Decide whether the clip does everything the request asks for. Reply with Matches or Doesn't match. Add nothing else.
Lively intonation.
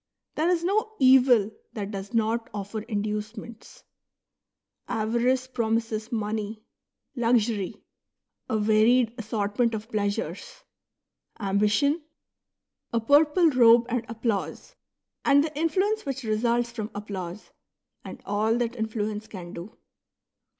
Doesn't match